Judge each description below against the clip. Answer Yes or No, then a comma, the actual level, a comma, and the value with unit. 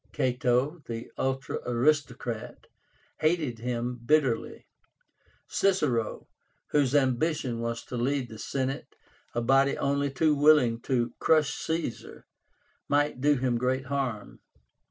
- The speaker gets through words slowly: Yes, slow, 115 wpm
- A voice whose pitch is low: Yes, low, 130 Hz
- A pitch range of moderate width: Yes, average, 3.3 semitones